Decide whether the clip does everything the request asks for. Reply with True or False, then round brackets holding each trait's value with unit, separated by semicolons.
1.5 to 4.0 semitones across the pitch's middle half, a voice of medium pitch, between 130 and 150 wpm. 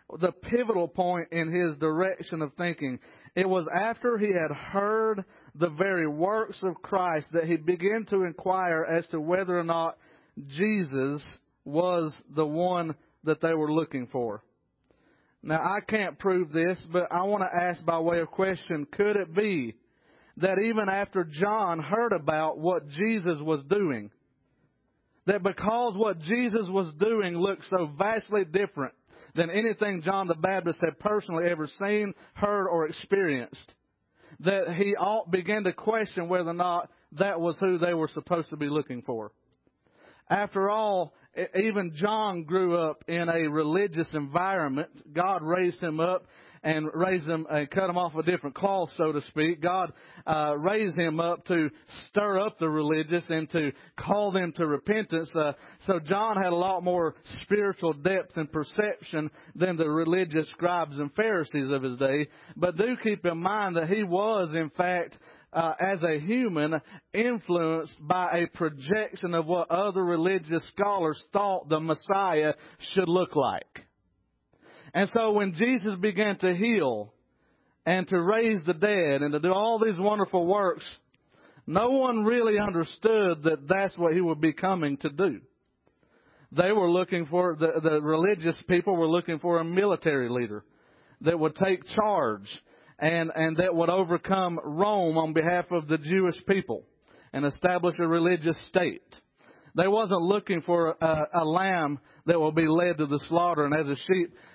False (3.4 semitones; 175 Hz; 160 wpm)